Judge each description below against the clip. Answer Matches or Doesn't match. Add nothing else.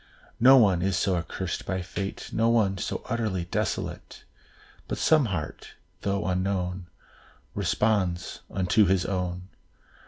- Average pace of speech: Doesn't match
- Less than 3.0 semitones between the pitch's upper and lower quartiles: Matches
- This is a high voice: Doesn't match